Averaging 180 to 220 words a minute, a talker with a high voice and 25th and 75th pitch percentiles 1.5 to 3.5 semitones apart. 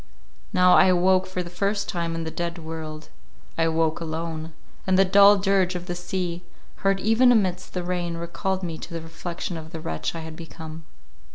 No: average, 185 wpm; medium, 175 Hz; narrow, 2.4 semitones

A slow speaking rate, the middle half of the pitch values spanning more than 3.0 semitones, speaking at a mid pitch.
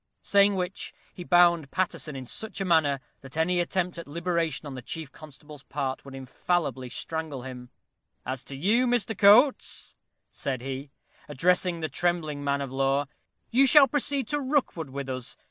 No: average, 165 wpm; average, 5.2 semitones; medium, 160 Hz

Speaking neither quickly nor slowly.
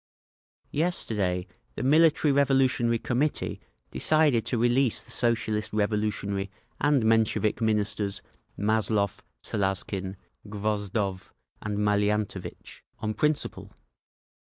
No: slow, 85 wpm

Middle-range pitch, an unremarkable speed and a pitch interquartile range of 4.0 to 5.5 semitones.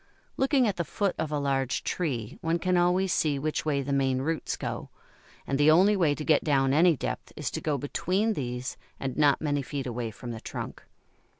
No: medium, 150 Hz; fast, 210 wpm; average, 4.3 semitones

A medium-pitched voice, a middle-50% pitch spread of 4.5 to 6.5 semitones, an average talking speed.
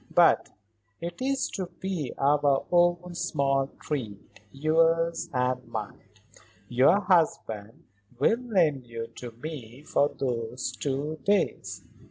No: medium, 145 Hz; wide, 5.5 semitones; slow, 115 wpm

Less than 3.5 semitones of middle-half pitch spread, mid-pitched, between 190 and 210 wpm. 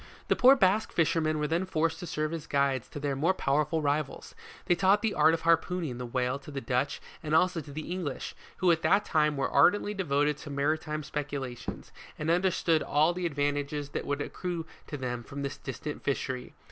Yes: average, 3.1 semitones; medium, 150 Hz; average, 200 wpm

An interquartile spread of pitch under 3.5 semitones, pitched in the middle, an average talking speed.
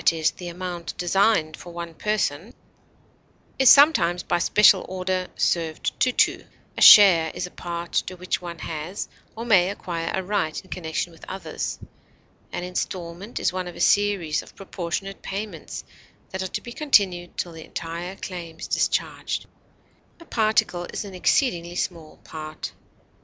Yes: narrow, 2.6 semitones; medium, 180 Hz; average, 160 wpm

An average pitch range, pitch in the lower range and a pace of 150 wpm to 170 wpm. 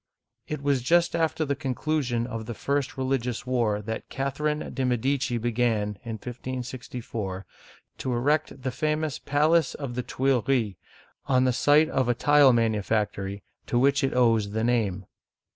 Yes: average, 3.5 semitones; low, 125 Hz; average, 160 wpm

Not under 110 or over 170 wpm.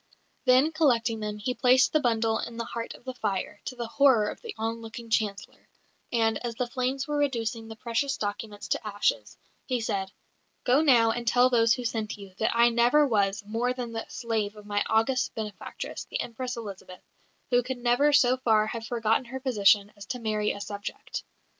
No: average, 195 wpm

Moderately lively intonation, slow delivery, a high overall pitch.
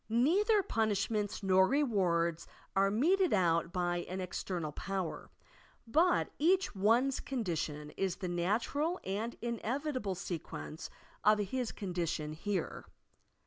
No: wide, 6.2 semitones; slow, 120 wpm; high, 200 Hz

